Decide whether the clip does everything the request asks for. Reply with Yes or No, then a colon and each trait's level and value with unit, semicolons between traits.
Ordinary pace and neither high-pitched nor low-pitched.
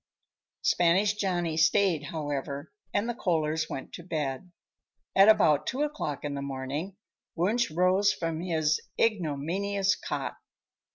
No: slow, 125 wpm; medium, 170 Hz